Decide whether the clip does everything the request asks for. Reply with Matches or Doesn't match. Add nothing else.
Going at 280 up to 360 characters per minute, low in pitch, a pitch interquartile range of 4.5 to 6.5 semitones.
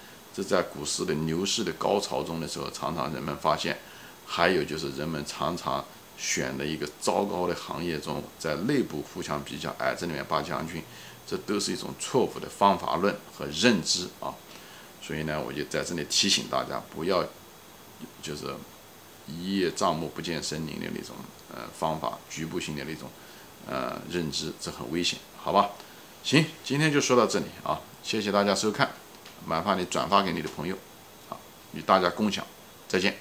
Doesn't match